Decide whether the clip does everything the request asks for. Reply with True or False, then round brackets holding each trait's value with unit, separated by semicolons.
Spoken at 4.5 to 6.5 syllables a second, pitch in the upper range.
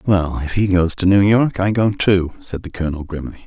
False (5.4 syllables/s; 90 Hz)